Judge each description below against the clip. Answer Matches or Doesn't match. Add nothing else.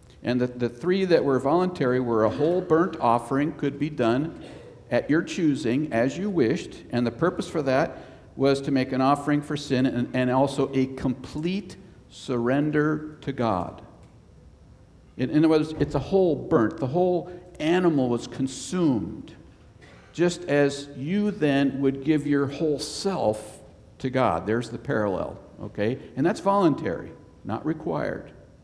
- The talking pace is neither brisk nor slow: Matches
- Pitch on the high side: Doesn't match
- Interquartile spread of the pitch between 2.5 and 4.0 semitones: Doesn't match